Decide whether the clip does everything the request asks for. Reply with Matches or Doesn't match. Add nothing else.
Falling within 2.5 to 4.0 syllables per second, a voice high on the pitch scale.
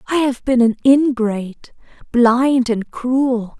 Matches